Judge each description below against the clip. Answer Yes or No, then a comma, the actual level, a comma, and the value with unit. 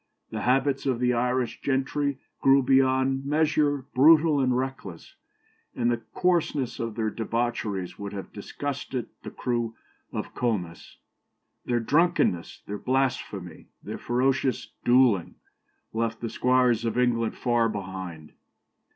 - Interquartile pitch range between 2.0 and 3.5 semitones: Yes, average, 3.1 semitones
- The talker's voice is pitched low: Yes, low, 125 Hz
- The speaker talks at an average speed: No, slow, 125 wpm